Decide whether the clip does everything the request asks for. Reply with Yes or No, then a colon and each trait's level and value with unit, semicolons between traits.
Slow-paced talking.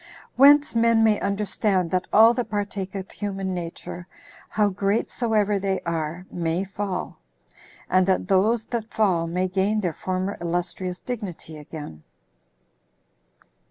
Yes: slow, 130 wpm